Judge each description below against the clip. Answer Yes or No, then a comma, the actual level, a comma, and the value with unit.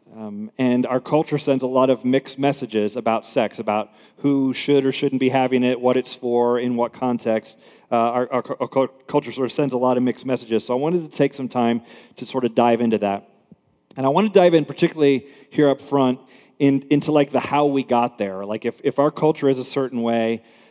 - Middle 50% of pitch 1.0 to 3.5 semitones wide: Yes, average, 2.9 semitones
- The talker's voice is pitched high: No, low, 130 Hz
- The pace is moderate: No, fast, 230 wpm